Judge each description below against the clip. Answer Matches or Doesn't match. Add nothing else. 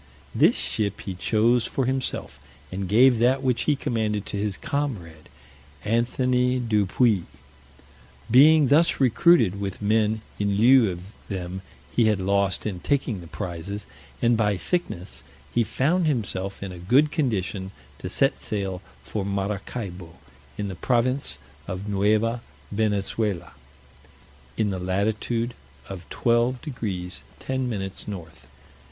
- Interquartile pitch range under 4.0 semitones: Doesn't match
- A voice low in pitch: Matches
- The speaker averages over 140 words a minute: Doesn't match